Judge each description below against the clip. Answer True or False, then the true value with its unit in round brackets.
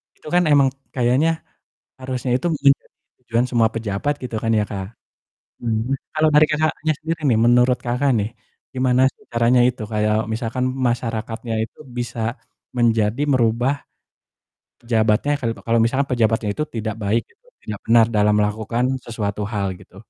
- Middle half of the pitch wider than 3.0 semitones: False (2.7 semitones)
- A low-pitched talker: True (120 Hz)